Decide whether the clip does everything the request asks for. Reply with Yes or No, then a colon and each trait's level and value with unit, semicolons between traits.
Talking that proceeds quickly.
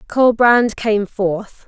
No: slow, 110 wpm